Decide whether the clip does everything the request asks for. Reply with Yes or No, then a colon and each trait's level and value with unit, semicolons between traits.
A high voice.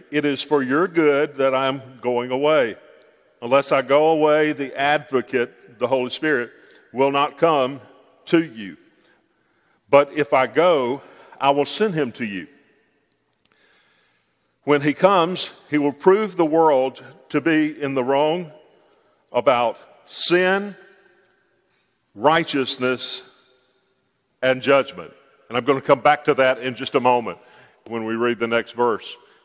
No: medium, 140 Hz